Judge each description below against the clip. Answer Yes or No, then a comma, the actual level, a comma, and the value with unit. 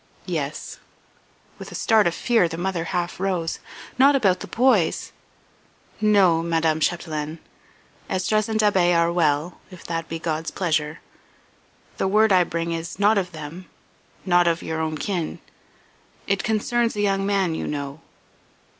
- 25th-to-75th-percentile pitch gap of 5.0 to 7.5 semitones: No, average, 3.4 semitones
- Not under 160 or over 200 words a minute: No, average, 150 wpm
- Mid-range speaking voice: Yes, medium, 175 Hz